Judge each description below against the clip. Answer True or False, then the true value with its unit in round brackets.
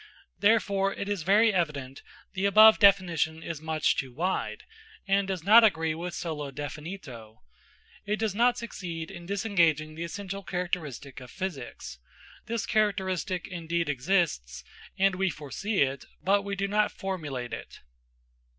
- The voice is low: False (180 Hz)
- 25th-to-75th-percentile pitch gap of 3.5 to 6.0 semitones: True (4.4 semitones)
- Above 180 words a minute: False (140 wpm)